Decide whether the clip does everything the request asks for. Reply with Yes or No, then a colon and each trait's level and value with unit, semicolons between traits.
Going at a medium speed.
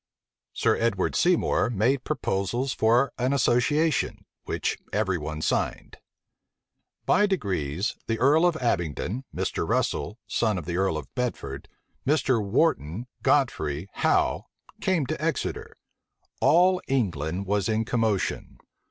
No: slow, 120 wpm